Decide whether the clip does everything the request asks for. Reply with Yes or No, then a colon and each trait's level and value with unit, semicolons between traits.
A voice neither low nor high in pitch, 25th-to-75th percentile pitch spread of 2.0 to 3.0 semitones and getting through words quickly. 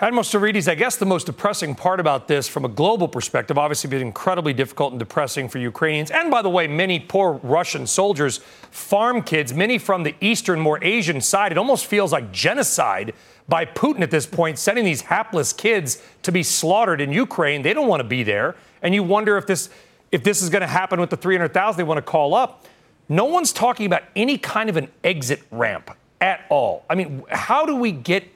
No: medium, 180 Hz; average, 5.0 semitones; fast, 215 wpm